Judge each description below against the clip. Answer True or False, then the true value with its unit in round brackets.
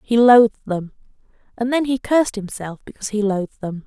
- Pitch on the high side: True (220 Hz)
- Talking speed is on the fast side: False (185 wpm)